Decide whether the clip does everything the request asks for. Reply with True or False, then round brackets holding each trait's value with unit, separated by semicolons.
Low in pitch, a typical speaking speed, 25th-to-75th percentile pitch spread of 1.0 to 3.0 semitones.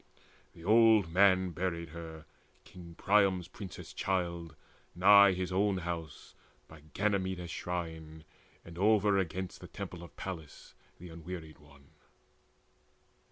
False (90 Hz; 115 wpm; 2.6 semitones)